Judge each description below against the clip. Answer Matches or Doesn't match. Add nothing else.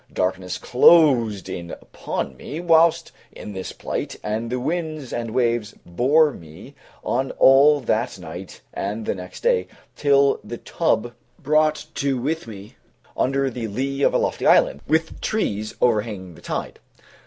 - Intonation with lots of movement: Matches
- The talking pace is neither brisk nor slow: Matches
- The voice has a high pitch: Doesn't match